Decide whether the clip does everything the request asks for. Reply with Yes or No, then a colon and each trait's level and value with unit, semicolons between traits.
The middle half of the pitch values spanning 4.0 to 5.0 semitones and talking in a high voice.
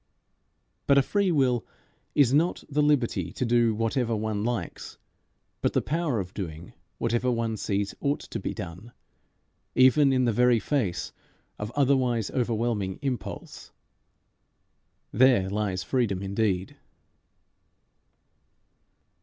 No: average, 4.3 semitones; low, 120 Hz